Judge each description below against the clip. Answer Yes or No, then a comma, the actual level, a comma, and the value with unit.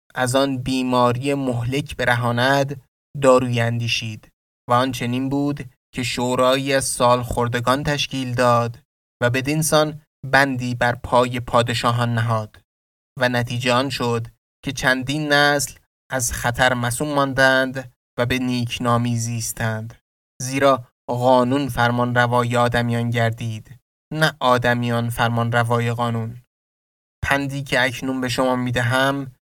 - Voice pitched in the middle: No, low, 125 Hz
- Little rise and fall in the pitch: Yes, narrow, 1.9 semitones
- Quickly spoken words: No, average, 115 wpm